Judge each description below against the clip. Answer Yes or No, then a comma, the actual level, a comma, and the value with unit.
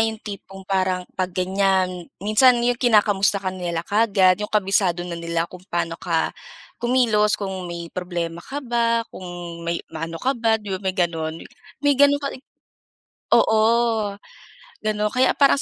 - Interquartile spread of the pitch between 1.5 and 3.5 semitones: No, average, 4.3 semitones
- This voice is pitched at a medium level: No, high, 195 Hz